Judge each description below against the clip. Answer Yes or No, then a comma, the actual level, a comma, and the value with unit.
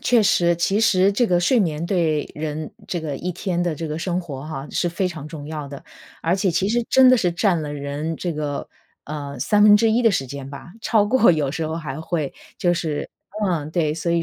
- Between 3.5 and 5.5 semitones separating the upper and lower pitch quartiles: Yes, average, 3.8 semitones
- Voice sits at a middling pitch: Yes, medium, 170 Hz